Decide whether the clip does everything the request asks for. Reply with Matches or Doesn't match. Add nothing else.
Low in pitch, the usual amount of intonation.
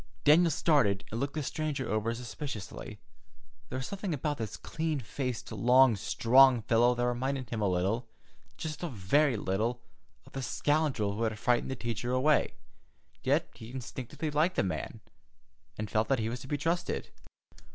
Matches